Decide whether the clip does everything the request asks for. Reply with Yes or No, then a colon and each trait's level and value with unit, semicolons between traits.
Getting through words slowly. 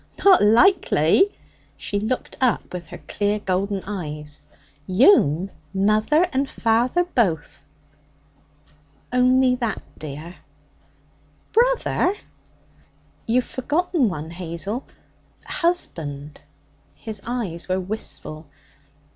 Yes: slow, 90 wpm